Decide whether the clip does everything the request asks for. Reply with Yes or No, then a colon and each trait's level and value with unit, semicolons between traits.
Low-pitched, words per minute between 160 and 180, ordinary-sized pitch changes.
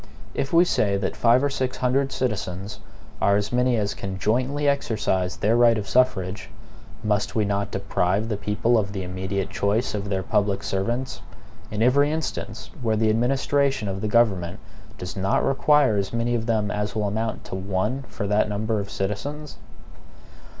Yes: low, 105 Hz; average, 175 wpm; average, 3.8 semitones